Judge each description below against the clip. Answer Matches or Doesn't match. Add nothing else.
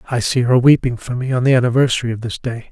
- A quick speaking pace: Matches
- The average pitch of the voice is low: Matches